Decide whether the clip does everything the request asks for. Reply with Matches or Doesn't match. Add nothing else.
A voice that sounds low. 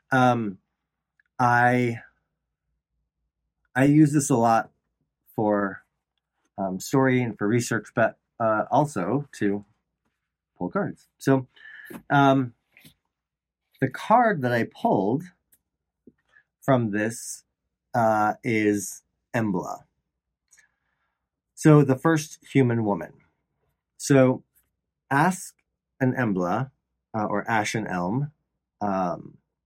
Matches